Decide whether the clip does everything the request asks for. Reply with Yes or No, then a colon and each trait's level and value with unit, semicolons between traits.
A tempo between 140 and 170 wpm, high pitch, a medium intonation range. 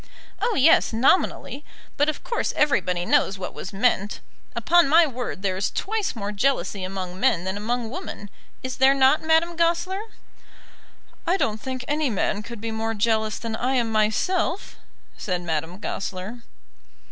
No: average, 160 wpm; high, 235 Hz; wide, 6.9 semitones